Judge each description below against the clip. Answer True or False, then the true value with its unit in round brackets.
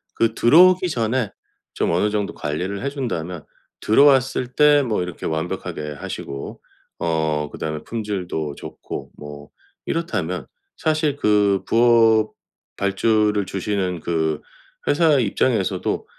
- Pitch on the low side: True (105 Hz)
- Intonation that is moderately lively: False (7.2 semitones)